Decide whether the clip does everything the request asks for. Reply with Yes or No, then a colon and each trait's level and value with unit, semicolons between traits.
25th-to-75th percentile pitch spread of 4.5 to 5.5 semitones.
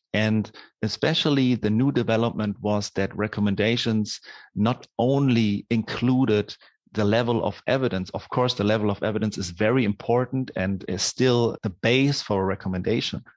No: average, 3.1 semitones